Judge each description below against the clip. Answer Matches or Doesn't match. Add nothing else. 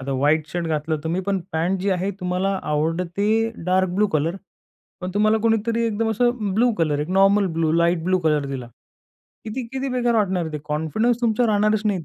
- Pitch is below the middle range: Doesn't match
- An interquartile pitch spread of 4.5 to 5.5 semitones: Matches